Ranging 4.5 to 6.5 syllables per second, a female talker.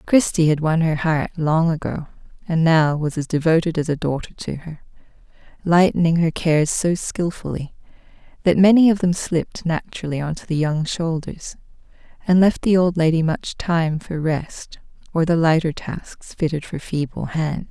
Yes: 4.8 syllables/s; female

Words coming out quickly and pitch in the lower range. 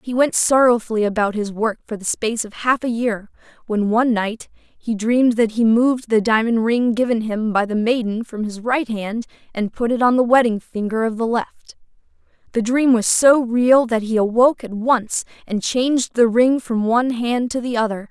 No: fast, 210 wpm; high, 230 Hz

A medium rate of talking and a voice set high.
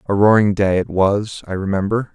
No: average, 195 wpm; low, 100 Hz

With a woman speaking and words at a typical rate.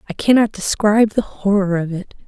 Yes: female; average, 185 wpm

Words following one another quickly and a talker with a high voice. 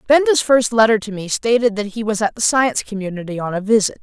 Yes: fast, 240 wpm; high, 220 Hz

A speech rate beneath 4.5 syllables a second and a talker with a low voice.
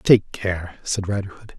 Yes: 4.0 syllables/s; very low, 95 Hz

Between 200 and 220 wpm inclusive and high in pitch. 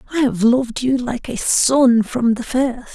Yes: fast, 205 wpm; high, 245 Hz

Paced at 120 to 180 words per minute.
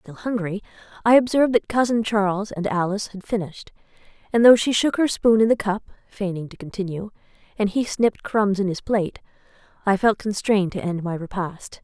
No: average, 190 wpm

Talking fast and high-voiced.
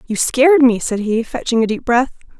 Yes: fast, 225 wpm; high, 245 Hz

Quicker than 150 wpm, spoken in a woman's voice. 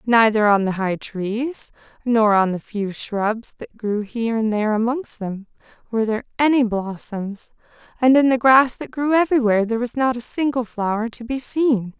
Yes: average, 185 wpm; female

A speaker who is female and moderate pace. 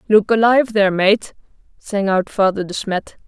Yes: female; average, 165 wpm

